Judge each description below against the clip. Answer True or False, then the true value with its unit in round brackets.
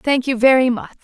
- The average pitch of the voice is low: False (255 Hz)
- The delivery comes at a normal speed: False (235 wpm)